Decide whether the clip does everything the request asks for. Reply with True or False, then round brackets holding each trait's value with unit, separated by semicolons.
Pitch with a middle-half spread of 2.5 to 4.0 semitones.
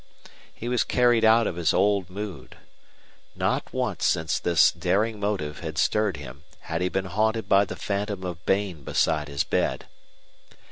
False (4.5 semitones)